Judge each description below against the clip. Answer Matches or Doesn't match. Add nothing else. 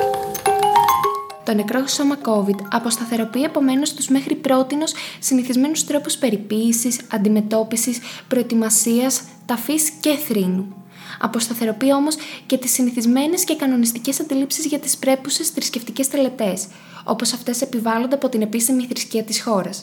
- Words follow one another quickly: Doesn't match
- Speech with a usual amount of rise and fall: Matches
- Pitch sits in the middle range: Doesn't match